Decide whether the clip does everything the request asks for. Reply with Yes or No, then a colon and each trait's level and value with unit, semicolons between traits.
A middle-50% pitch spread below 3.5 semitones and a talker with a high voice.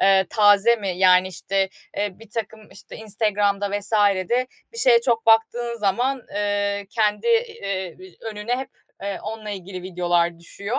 Yes: average, 2.8 semitones; high, 205 Hz